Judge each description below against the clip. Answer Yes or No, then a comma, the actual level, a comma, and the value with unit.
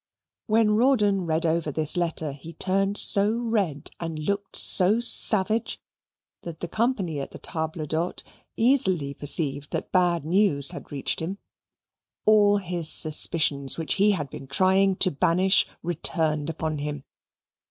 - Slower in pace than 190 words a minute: Yes, average, 140 wpm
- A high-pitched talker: No, medium, 170 Hz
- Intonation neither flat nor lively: Yes, average, 4.5 semitones